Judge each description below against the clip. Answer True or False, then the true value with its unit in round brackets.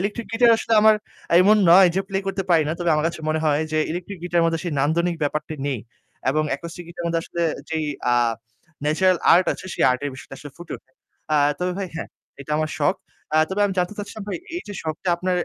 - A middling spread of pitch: True (3.5 semitones)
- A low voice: False (170 Hz)